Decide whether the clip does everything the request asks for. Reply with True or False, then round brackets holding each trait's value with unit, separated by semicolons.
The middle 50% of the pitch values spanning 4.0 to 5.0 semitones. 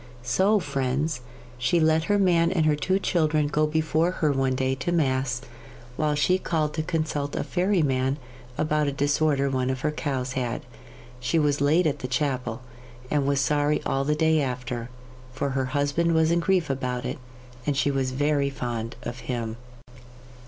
False (3.2 semitones)